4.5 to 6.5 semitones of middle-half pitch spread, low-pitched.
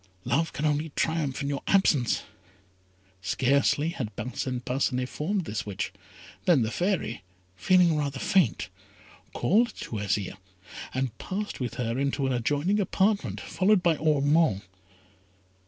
No: wide, 5.5 semitones; medium, 145 Hz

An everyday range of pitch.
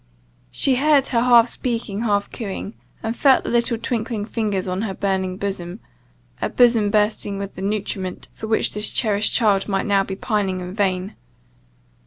Yes: average, 3.1 semitones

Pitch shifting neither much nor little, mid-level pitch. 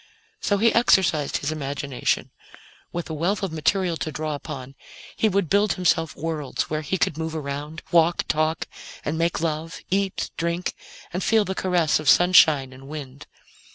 Yes: average, 3.4 semitones; medium, 160 Hz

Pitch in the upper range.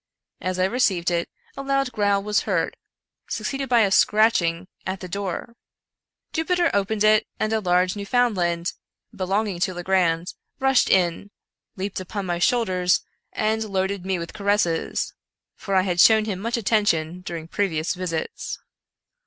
Yes: high, 195 Hz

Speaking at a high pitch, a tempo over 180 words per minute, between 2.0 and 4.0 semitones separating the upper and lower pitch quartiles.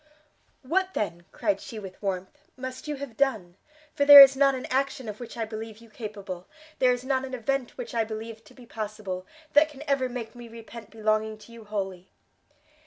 Yes: high, 230 Hz; average, 200 wpm; average, 3.7 semitones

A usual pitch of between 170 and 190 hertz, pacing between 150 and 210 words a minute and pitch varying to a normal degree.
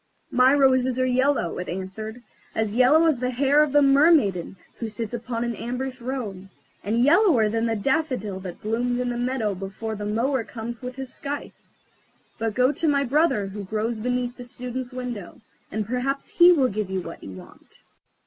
No: high, 245 Hz; average, 185 wpm; average, 3.6 semitones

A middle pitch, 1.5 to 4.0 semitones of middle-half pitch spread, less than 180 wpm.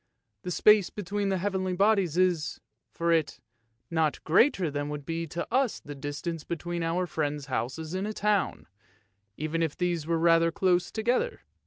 Yes: medium, 170 Hz; average, 3.3 semitones; average, 165 wpm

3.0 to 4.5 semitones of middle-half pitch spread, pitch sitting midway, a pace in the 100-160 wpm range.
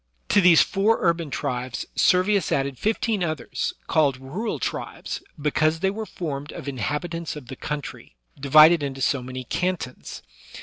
No: average, 4.9 semitones; medium, 155 Hz; average, 150 wpm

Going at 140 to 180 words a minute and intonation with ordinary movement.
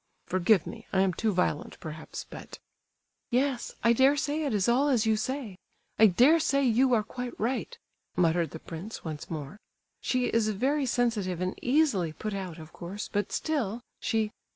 No: average, 175 wpm; wide, 5.8 semitones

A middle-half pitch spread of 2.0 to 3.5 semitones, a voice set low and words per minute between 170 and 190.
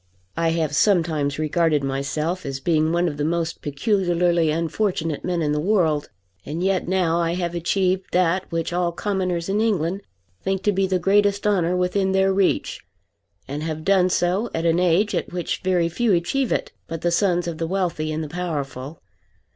No: average, 2.9 semitones; medium, 175 Hz; average, 185 wpm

